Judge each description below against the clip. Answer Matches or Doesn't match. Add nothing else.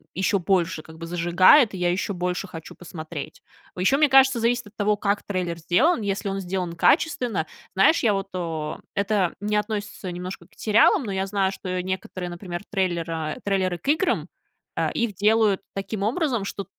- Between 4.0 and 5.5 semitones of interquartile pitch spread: Doesn't match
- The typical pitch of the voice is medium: Doesn't match